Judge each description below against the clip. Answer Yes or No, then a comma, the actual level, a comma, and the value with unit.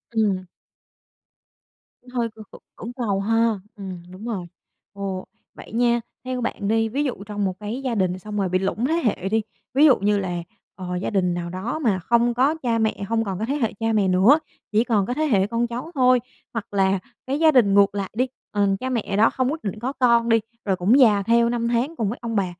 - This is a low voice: No, high, 220 Hz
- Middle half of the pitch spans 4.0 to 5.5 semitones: No, average, 3.6 semitones